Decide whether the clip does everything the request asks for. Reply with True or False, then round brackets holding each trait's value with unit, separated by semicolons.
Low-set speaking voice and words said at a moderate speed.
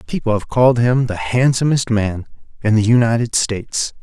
True (115 Hz; 165 wpm)